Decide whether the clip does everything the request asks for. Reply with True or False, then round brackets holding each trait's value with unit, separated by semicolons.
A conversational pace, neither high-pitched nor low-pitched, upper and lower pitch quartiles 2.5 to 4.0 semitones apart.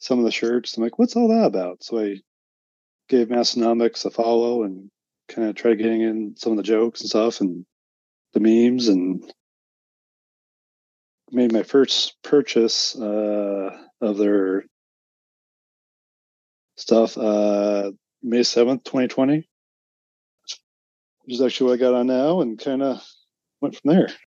False (145 wpm; 115 Hz; 3.2 semitones)